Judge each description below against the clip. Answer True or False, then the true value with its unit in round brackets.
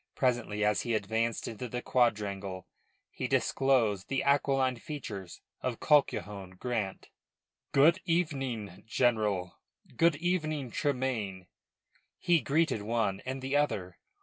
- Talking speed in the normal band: False (115 wpm)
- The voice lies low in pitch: True (120 Hz)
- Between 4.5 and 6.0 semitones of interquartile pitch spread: True (5.1 semitones)